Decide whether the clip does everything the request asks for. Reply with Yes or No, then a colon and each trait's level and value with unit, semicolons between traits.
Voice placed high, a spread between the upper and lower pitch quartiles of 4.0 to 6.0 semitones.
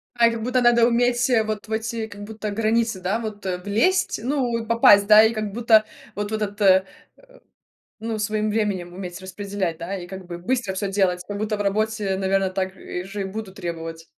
No: high, 210 Hz; average, 2.8 semitones